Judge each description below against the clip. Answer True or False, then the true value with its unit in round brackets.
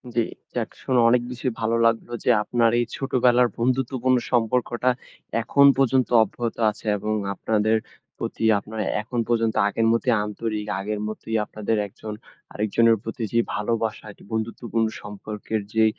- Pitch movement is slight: True (2.0 semitones)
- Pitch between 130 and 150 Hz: False (115 Hz)